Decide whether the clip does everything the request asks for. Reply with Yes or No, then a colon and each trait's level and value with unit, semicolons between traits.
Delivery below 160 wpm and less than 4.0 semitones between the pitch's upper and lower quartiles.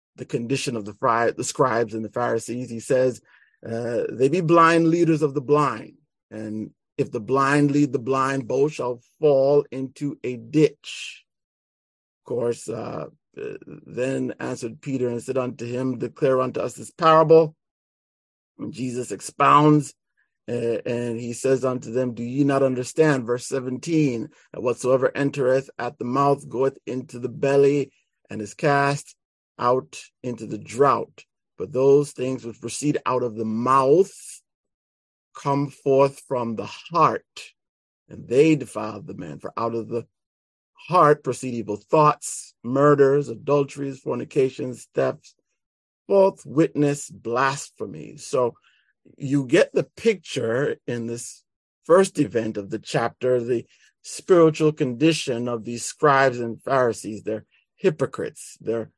Yes: average, 140 wpm; average, 3.6 semitones